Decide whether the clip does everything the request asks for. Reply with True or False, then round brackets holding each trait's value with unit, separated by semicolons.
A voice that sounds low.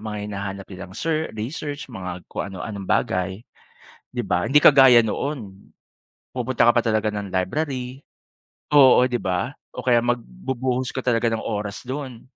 True (115 Hz)